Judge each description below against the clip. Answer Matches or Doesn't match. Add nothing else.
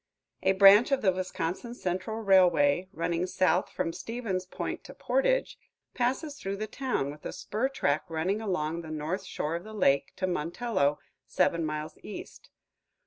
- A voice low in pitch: Doesn't match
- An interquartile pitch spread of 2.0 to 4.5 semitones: Doesn't match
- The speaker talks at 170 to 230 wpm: Doesn't match